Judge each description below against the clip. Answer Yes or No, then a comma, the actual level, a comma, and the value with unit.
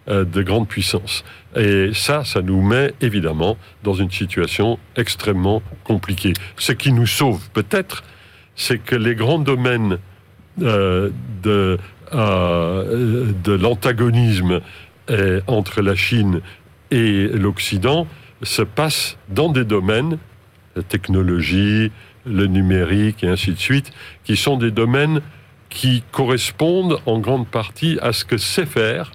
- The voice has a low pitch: Yes, low, 105 Hz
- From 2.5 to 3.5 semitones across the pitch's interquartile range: No, average, 4.2 semitones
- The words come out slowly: Yes, slow, 120 wpm